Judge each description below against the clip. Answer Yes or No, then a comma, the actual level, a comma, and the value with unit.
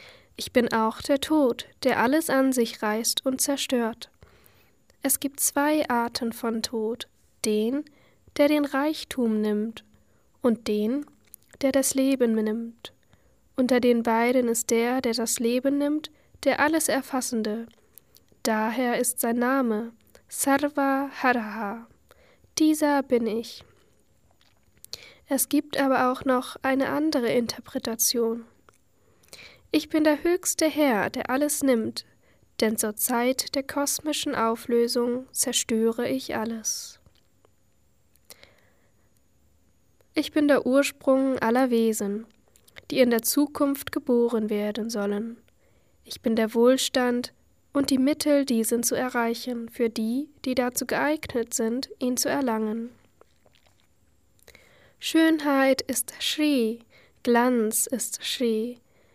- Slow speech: Yes, slow, 115 wpm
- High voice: Yes, very high, 250 Hz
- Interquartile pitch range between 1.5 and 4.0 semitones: Yes, average, 3.3 semitones